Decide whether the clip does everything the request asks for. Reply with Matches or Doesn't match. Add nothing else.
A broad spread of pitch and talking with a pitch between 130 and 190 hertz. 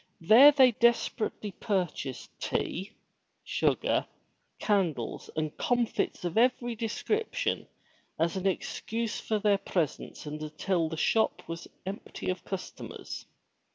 Doesn't match